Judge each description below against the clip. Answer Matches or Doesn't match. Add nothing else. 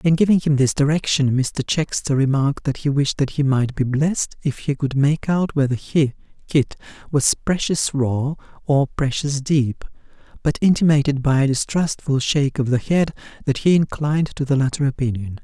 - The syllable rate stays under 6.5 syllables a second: Matches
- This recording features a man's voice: Matches